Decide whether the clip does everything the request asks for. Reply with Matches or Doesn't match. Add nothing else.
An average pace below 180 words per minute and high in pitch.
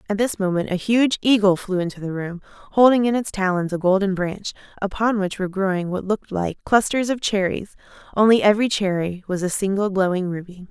Doesn't match